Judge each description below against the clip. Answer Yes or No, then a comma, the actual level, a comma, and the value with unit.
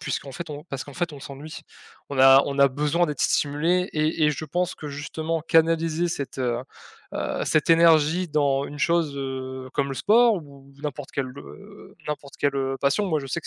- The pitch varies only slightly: No, average, 3.1 semitones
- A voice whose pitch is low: No, medium, 150 Hz